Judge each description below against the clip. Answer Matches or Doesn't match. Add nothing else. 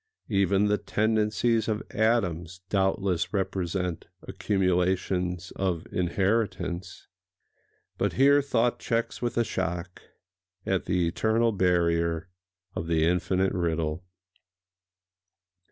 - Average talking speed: Doesn't match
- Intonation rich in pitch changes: Doesn't match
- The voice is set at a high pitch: Doesn't match